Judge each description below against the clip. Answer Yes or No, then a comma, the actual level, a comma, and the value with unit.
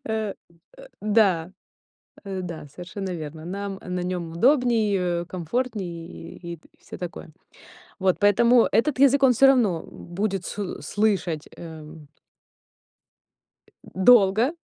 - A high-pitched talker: Yes, high, 195 Hz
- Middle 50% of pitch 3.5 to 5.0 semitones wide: Yes, average, 4.4 semitones